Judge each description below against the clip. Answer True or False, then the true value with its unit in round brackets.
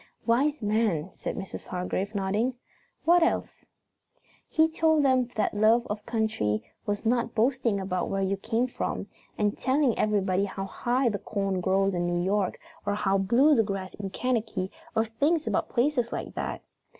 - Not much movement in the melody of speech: False (4.2 semitones)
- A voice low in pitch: False (215 Hz)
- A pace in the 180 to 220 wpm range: False (170 wpm)